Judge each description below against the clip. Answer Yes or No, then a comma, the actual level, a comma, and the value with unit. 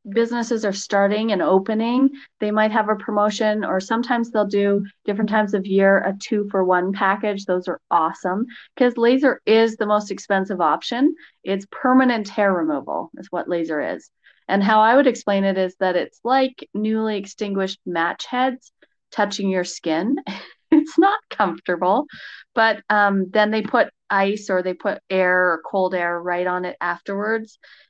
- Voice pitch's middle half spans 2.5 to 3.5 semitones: Yes, average, 3.2 semitones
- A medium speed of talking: Yes, average, 170 wpm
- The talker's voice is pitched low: No, high, 210 Hz